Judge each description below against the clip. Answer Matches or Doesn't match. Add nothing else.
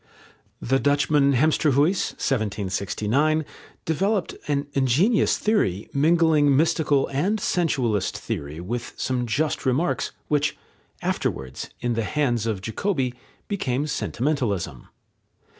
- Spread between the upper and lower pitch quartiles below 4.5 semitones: Doesn't match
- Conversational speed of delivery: Doesn't match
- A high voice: Doesn't match